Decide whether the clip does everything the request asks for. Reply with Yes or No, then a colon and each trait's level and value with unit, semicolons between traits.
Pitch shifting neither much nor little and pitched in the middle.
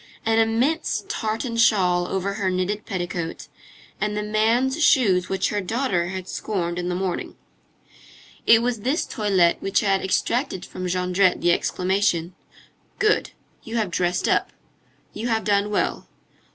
No: average, 3.6 semitones; high, 200 Hz